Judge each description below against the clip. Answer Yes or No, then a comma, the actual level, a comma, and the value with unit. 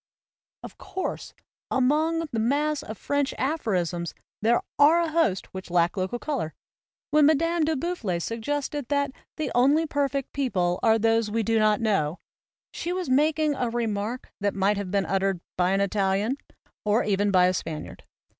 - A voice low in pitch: No, high, 230 Hz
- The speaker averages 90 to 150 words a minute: No, average, 165 wpm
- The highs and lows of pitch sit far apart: Yes, wide, 6.8 semitones